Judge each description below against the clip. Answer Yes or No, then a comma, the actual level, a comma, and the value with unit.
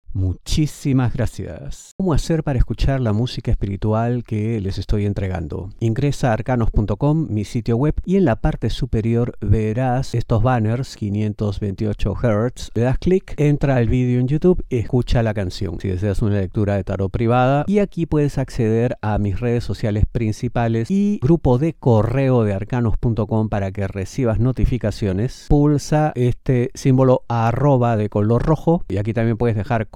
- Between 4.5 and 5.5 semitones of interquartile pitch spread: No, average, 3.8 semitones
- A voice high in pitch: No, low, 120 Hz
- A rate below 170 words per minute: Yes, average, 160 wpm